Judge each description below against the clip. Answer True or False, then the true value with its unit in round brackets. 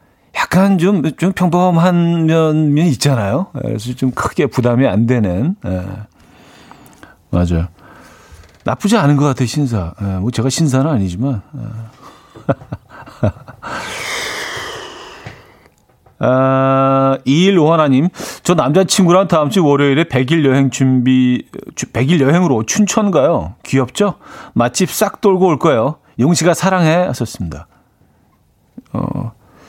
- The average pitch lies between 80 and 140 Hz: True (135 Hz)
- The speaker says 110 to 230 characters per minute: True (220 characters per minute)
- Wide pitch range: True (5.7 semitones)